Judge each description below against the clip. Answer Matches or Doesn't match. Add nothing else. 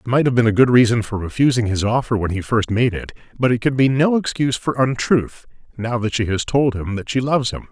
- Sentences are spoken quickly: Matches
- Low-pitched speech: Matches